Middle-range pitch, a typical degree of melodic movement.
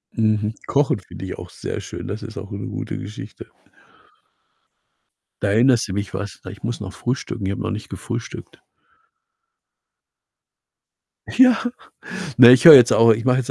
No: low, 115 Hz; average, 3.4 semitones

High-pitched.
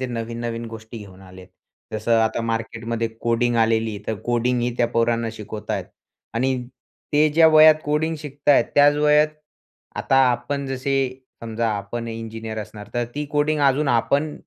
No: low, 120 Hz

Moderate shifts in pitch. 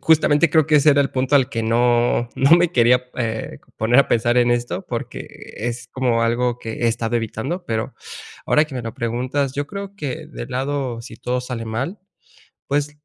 Yes: average, 3.5 semitones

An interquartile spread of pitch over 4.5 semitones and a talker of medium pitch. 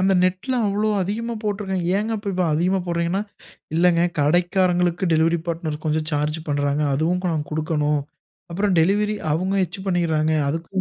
No: average, 3.4 semitones; medium, 175 Hz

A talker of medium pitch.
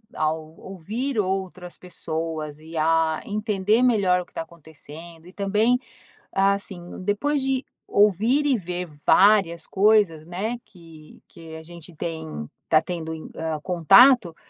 Yes: medium, 180 Hz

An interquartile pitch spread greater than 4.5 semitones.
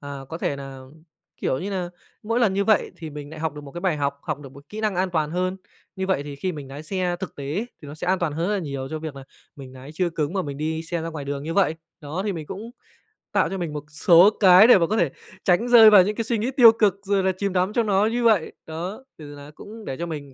Yes: average, 5.1 semitones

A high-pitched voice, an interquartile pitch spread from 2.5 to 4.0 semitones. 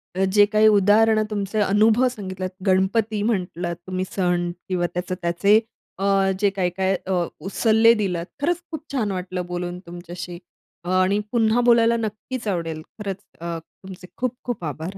Yes: high, 195 Hz; average, 3.3 semitones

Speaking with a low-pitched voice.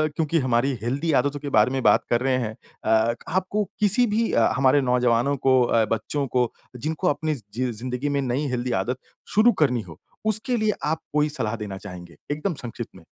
Yes: low, 130 Hz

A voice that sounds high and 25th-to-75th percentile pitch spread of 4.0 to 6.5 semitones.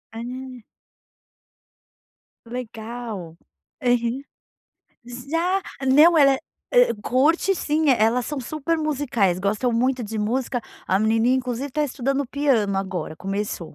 Yes: high, 245 Hz; average, 4.3 semitones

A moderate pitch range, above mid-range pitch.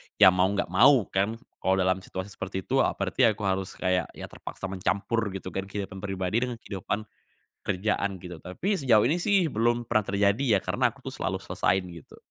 No: average, 3.5 semitones; low, 100 Hz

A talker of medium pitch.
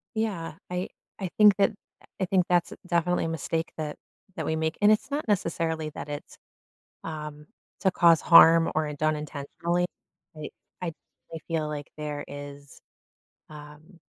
Yes: medium, 160 Hz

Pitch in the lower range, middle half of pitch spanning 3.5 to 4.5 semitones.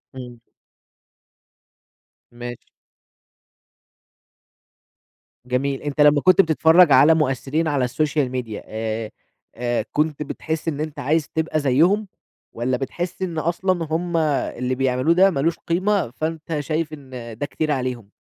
No: medium, 150 Hz; average, 4.2 semitones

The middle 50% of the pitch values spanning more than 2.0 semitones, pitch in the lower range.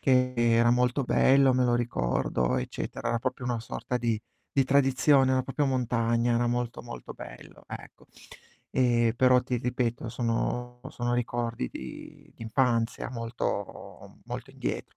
No: narrow, 1.5 semitones; low, 120 Hz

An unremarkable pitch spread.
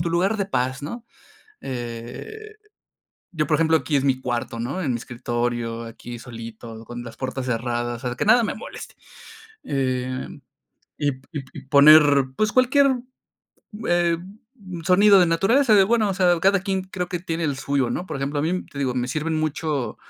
No: wide, 6.8 semitones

